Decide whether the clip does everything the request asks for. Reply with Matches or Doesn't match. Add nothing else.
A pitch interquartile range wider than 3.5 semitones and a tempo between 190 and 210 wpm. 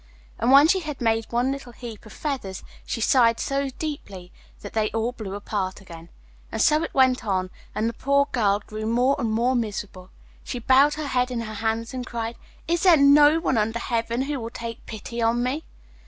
Matches